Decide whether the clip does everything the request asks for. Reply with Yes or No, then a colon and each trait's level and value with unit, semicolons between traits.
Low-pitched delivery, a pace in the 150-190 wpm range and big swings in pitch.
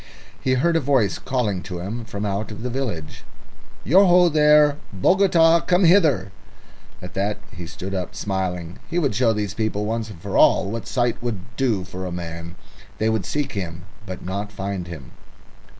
Yes: low, 105 Hz; average, 180 wpm; wide, 6.3 semitones